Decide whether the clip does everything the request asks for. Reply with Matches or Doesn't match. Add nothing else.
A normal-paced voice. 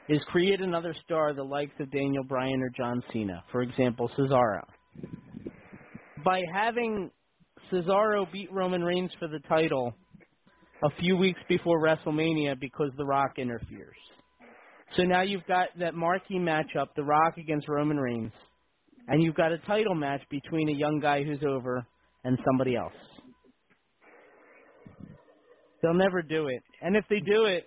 Matches